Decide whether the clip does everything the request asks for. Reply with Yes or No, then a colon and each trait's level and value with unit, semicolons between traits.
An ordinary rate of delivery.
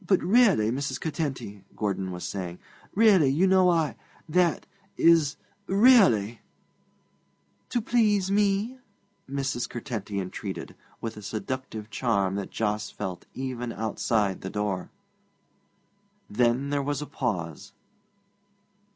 No: slow, 115 wpm